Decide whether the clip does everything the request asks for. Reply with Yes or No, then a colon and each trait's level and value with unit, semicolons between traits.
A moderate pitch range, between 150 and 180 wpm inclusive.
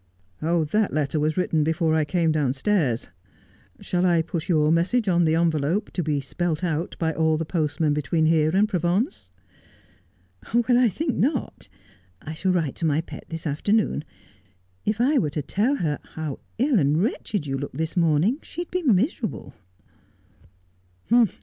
Yes: average, 4.7 semitones; average, 170 wpm